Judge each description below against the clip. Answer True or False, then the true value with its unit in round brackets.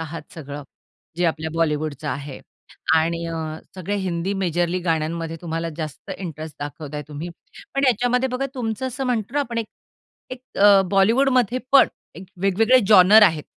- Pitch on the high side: False (180 Hz)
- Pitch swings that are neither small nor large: False (6.2 semitones)